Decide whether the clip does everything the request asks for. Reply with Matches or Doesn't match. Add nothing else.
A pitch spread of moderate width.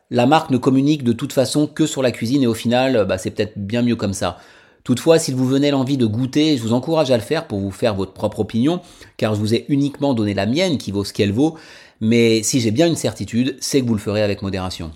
Matches